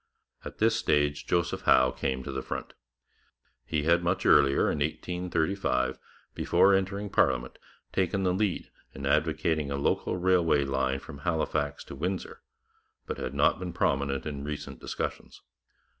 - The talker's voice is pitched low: Yes, very low, 75 Hz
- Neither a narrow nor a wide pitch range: Yes, average, 4.4 semitones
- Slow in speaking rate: No, average, 145 wpm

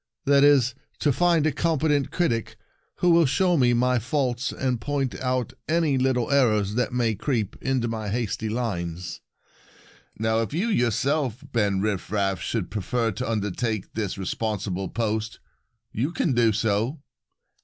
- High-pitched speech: No, low, 120 Hz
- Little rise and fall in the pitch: No, average, 4.4 semitones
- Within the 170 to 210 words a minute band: No, average, 150 wpm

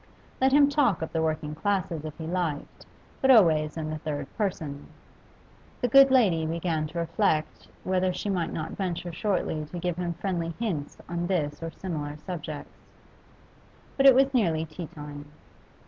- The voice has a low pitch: No, medium, 170 Hz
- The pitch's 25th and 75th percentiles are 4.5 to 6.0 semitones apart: No, average, 3.7 semitones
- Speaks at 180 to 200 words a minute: No, average, 165 wpm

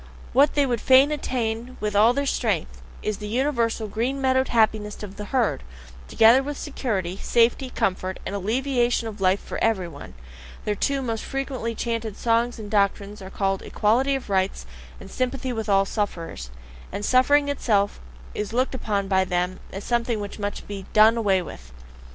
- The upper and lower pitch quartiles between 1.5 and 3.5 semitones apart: No, average, 4.1 semitones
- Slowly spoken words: No, average, 175 wpm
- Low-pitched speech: No, high, 225 Hz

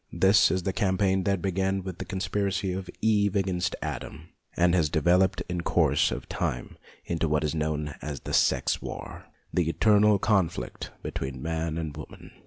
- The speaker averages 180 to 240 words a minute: No, average, 170 wpm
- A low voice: Yes, very low, 90 Hz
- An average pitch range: Yes, average, 3.2 semitones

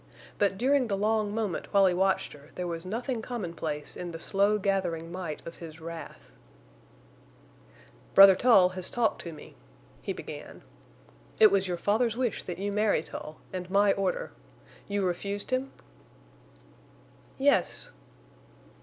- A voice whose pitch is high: Yes, high, 195 Hz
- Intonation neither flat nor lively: Yes, average, 3.4 semitones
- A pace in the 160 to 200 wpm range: No, average, 145 wpm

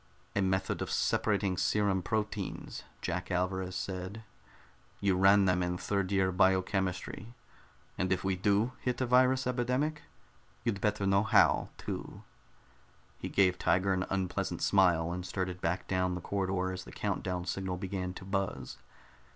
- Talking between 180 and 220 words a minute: No, average, 150 wpm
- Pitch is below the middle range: Yes, very low, 95 Hz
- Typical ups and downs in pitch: No, narrow, 1.8 semitones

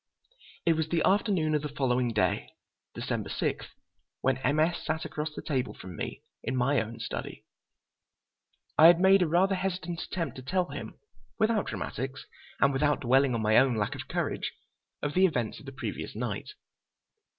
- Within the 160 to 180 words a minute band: Yes, average, 175 wpm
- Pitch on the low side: No, medium, 150 Hz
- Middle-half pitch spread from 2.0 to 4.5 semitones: No, average, 5.1 semitones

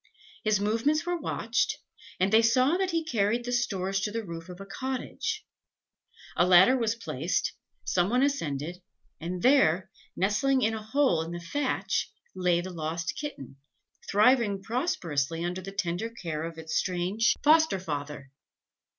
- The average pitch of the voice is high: Yes, high, 195 Hz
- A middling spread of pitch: No, wide, 5.9 semitones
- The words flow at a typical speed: Yes, average, 155 wpm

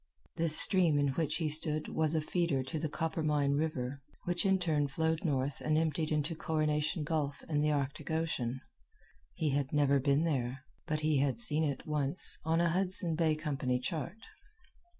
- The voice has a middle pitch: Yes, medium, 155 Hz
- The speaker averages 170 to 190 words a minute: Yes, average, 175 wpm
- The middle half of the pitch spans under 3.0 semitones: Yes, narrow, 2.4 semitones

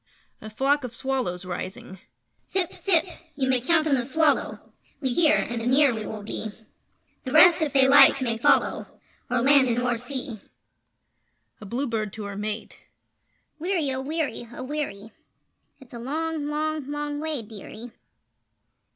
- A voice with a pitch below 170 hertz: No, very high, 260 Hz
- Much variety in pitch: No, average, 4.5 semitones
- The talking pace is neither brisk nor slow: Yes, average, 155 wpm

